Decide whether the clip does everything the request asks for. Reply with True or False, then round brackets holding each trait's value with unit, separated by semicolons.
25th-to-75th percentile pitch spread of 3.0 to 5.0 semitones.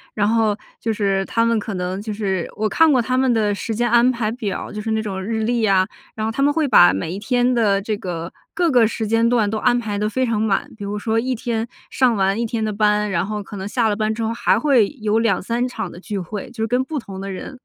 False (2.6 semitones)